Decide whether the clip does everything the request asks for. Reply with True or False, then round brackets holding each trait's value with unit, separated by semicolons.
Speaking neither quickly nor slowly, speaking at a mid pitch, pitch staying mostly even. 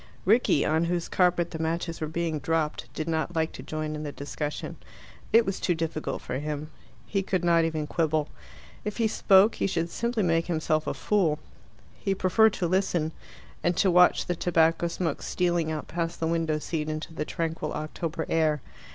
True (185 wpm; 165 Hz; 2.3 semitones)